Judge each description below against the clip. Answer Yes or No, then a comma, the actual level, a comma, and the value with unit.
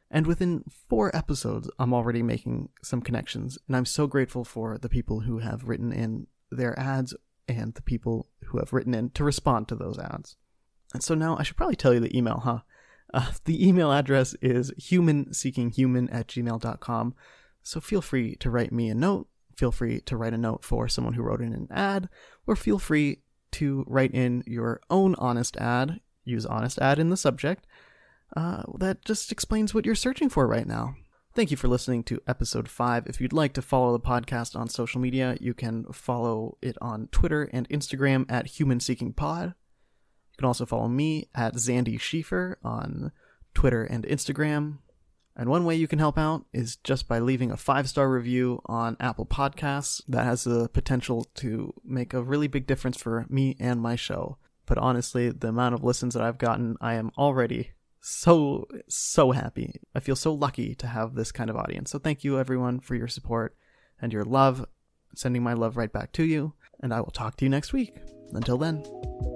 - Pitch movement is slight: No, average, 3.3 semitones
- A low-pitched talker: Yes, low, 125 Hz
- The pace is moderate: Yes, average, 195 wpm